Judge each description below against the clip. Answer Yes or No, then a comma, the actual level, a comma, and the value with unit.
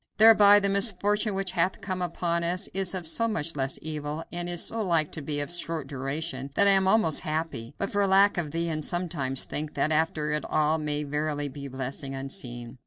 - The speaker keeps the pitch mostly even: No, average, 4.5 semitones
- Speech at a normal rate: No, fast, 220 wpm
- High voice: No, medium, 160 Hz